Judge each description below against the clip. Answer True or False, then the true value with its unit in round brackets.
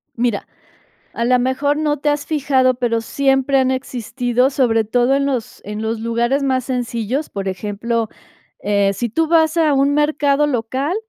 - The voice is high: True (255 Hz)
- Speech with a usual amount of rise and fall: True (3.4 semitones)